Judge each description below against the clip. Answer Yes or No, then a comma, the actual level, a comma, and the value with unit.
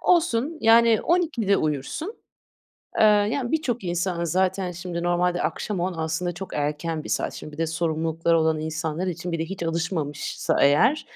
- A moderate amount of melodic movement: Yes, average, 4.6 semitones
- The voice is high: No, medium, 175 Hz